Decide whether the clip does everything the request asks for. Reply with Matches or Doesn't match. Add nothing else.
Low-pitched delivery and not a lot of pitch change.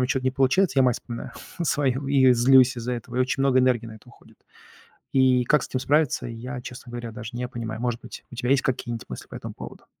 Matches